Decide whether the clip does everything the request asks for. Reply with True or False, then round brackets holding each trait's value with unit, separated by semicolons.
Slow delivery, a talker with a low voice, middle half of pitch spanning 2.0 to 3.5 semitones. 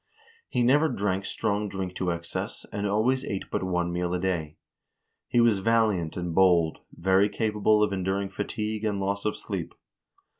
False (165 wpm; 100 Hz; 2.9 semitones)